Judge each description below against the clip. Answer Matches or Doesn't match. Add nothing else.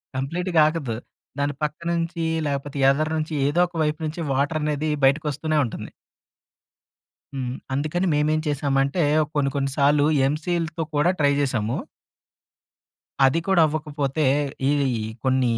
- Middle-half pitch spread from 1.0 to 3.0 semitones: Matches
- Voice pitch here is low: Doesn't match